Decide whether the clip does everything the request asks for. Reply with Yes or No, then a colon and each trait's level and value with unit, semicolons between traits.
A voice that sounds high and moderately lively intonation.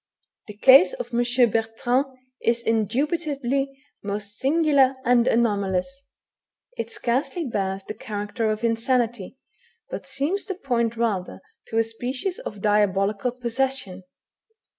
Yes: high, 235 Hz; average, 4.2 semitones